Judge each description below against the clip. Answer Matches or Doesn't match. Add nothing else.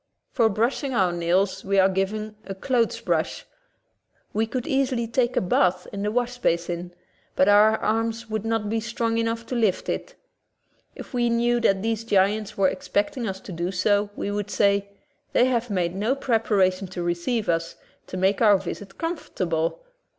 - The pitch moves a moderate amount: Matches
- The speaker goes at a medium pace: Matches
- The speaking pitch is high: Matches